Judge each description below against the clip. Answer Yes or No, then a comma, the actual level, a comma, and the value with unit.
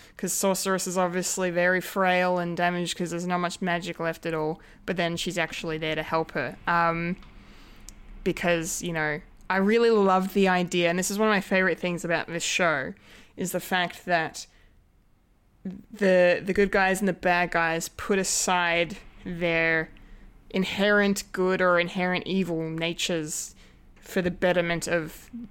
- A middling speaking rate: Yes, average, 160 wpm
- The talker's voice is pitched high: No, medium, 180 Hz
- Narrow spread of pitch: Yes, narrow, 2.1 semitones